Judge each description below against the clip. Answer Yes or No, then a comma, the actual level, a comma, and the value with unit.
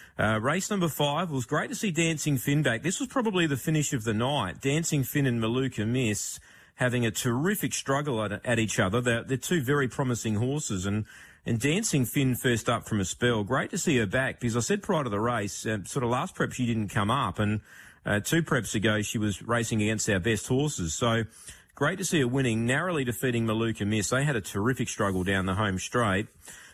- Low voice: Yes, low, 125 Hz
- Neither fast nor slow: No, fast, 225 wpm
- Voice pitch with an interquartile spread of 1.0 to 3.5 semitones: No, average, 4.8 semitones